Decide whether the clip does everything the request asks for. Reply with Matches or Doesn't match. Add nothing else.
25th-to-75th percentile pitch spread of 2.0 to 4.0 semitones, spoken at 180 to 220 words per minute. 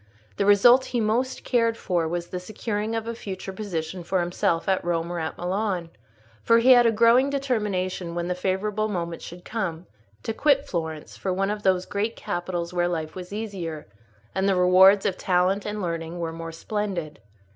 Matches